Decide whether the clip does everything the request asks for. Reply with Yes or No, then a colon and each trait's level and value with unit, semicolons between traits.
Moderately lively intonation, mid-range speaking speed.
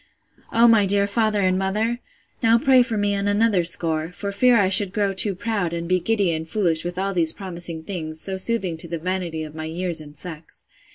No: average, 3.5 semitones; fast, 220 wpm